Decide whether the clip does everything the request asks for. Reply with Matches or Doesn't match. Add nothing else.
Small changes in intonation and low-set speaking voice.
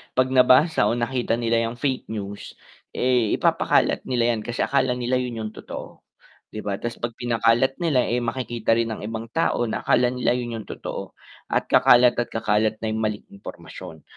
Matches